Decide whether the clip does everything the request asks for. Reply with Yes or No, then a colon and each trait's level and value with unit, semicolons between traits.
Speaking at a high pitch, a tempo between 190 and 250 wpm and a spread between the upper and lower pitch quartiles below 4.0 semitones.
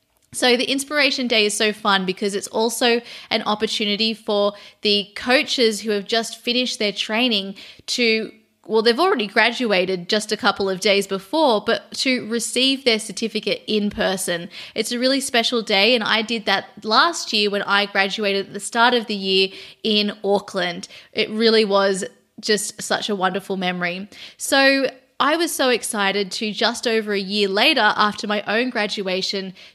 No: high, 215 Hz; average, 170 wpm; average, 2.7 semitones